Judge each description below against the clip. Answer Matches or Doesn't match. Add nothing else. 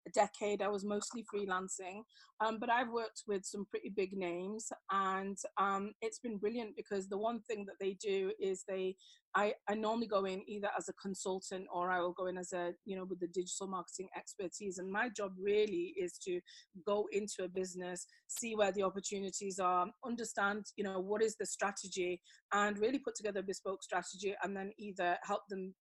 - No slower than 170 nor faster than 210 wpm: Matches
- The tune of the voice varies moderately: Doesn't match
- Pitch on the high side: Matches